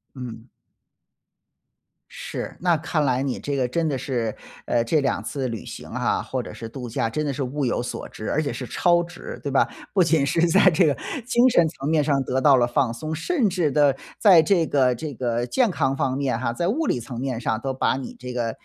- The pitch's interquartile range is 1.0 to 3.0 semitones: No, average, 4.4 semitones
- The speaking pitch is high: No, low, 135 Hz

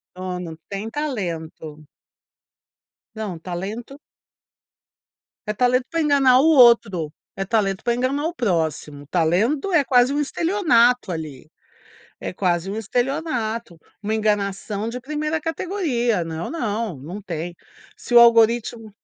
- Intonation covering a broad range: Yes, wide, 6.1 semitones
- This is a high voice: Yes, high, 225 Hz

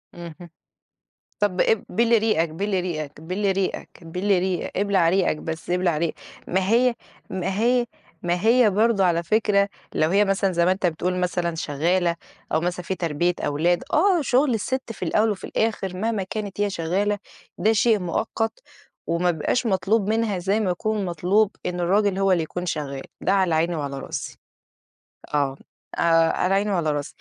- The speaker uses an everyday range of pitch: Yes, average, 3.5 semitones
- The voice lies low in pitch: No, medium, 185 Hz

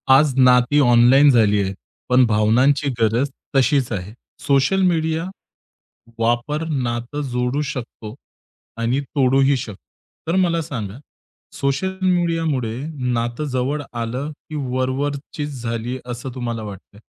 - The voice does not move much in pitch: No, average, 3.6 semitones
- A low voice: Yes, low, 130 Hz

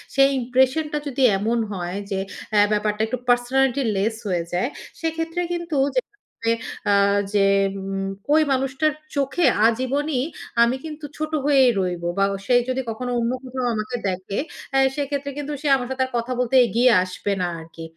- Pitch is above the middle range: Yes, very high, 250 Hz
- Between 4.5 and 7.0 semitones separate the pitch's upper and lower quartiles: Yes, average, 5.3 semitones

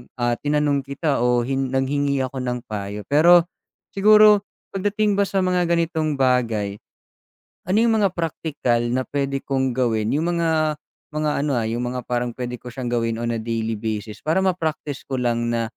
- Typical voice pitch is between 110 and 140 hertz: Yes, low, 135 Hz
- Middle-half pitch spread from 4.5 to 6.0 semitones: Yes, average, 5.3 semitones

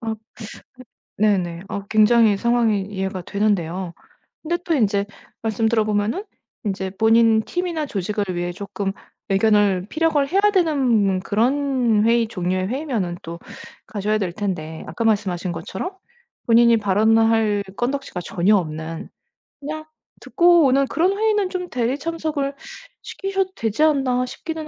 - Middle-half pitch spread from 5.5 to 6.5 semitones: Yes, wide, 6.1 semitones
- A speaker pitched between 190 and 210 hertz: No, high, 220 Hz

